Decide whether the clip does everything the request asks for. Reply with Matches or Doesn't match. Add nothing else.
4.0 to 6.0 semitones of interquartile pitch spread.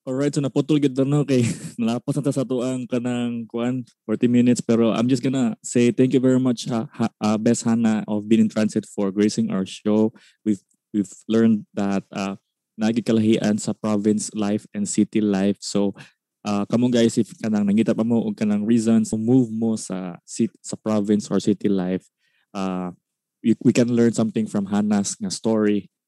Doesn't match